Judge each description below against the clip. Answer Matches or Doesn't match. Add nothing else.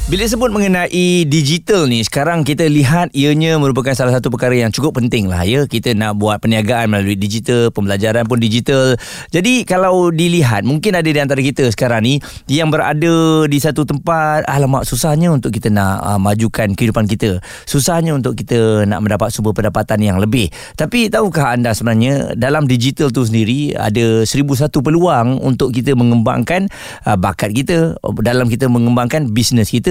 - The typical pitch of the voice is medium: Doesn't match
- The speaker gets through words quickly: Matches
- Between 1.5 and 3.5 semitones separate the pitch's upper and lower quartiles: Doesn't match